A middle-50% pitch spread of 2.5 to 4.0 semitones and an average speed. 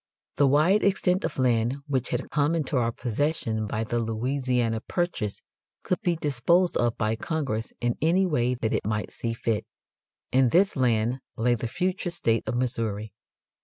No: wide, 5.5 semitones; average, 165 wpm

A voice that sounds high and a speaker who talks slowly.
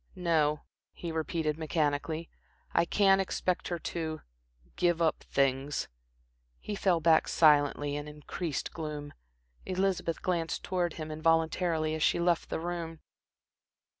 No: medium, 160 Hz; slow, 125 wpm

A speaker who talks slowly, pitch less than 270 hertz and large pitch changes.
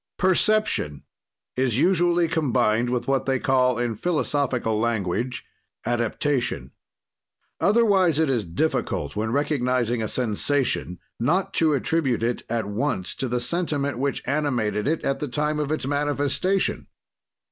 No: slow, 130 wpm; low, 135 Hz; average, 4.5 semitones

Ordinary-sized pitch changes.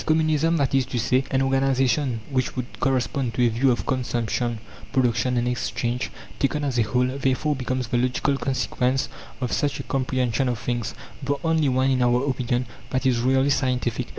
No: narrow, 1.7 semitones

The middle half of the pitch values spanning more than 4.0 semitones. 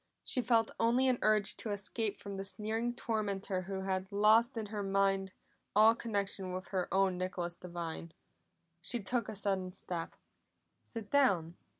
No: average, 2.9 semitones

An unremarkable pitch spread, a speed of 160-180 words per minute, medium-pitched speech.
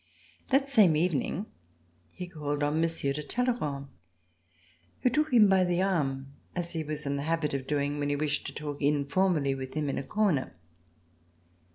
Yes: average, 4.5 semitones; average, 175 wpm; medium, 150 Hz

